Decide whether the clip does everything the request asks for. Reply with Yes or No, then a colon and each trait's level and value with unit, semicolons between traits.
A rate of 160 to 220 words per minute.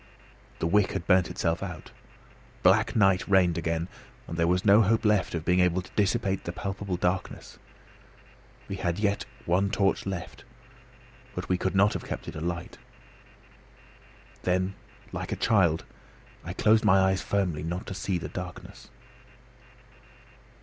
No: average, 150 wpm